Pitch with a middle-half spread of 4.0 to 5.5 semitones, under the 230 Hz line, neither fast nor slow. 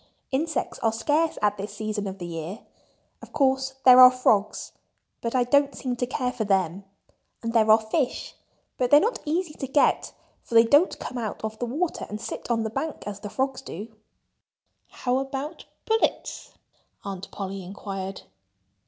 No: average, 4.5 semitones; high, 235 Hz; average, 170 wpm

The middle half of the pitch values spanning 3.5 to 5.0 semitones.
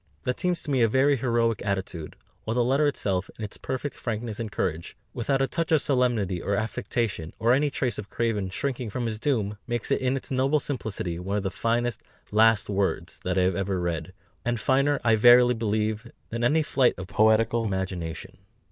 Yes: average, 4.2 semitones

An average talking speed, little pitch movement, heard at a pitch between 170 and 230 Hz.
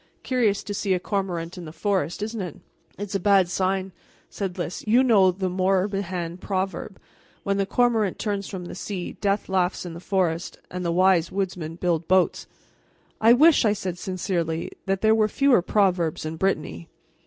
Yes: average, 175 wpm; narrow, 2.3 semitones; high, 190 Hz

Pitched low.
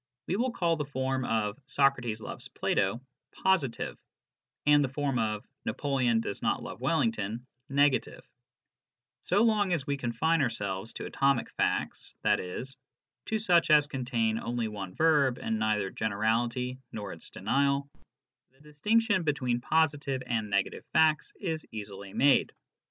Yes: low, 130 Hz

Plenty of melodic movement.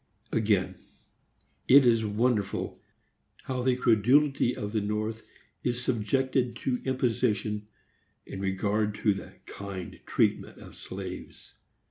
No: average, 3.4 semitones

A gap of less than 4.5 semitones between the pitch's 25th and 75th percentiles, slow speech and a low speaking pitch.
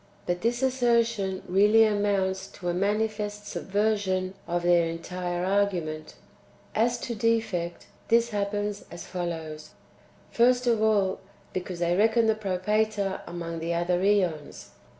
No: average, 3.6 semitones; slow, 130 wpm; high, 200 Hz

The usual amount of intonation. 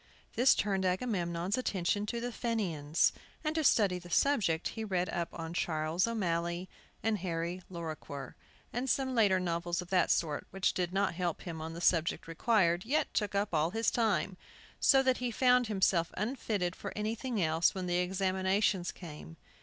Yes: average, 4.4 semitones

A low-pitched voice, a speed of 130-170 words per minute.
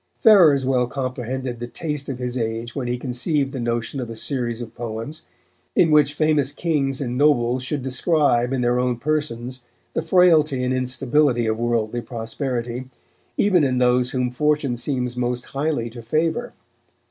Yes: low, 130 Hz; average, 165 wpm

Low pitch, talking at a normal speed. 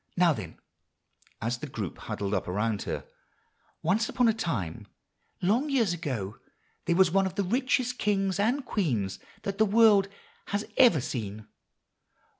No: high, 190 Hz; average, 150 wpm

